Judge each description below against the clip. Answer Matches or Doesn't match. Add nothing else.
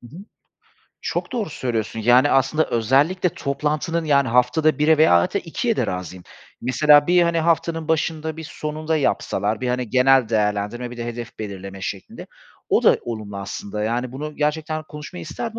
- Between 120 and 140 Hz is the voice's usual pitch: Matches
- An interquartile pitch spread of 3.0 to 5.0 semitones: Doesn't match